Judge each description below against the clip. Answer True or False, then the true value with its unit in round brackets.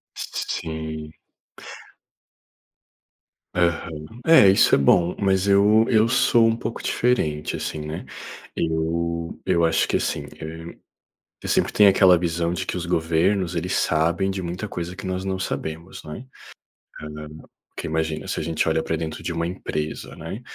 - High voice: False (85 Hz)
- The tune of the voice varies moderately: True (3.1 semitones)